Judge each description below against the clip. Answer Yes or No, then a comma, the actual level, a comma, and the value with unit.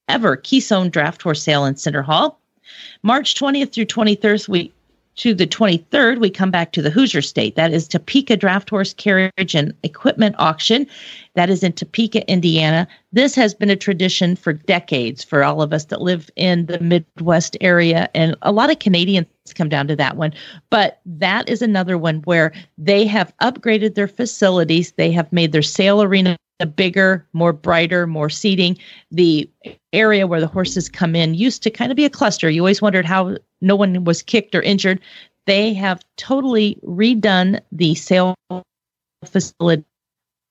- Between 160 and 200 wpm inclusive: Yes, average, 175 wpm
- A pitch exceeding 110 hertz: Yes, medium, 185 Hz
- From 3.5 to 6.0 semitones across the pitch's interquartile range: Yes, average, 4.1 semitones